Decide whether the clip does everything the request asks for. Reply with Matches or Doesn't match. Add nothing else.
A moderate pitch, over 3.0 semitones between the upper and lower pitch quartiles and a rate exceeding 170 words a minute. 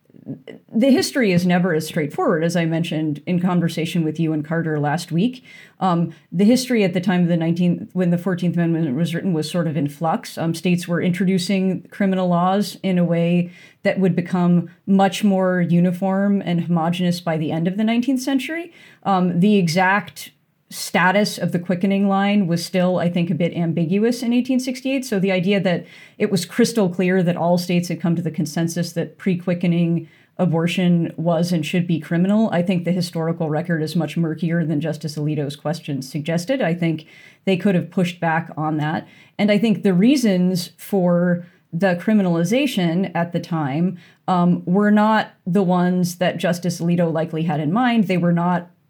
Doesn't match